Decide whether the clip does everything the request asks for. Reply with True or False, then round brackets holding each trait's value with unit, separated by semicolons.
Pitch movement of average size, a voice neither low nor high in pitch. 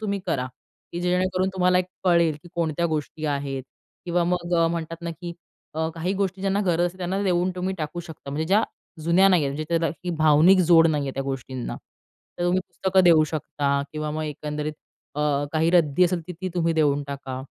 True (3.0 semitones; 165 Hz)